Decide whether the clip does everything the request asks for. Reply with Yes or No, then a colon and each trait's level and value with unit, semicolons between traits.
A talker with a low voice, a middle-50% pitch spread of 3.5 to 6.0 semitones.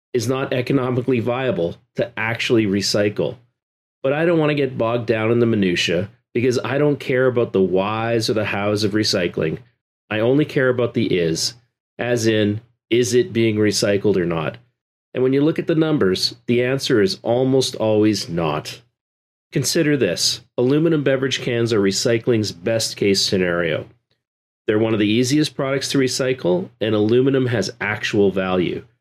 Yes: low, 120 Hz; average, 3.8 semitones